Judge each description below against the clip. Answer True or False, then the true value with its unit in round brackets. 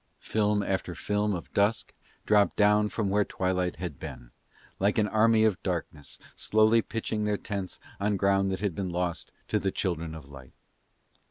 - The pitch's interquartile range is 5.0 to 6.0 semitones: False (2.7 semitones)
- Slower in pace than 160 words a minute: False (170 wpm)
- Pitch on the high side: False (100 Hz)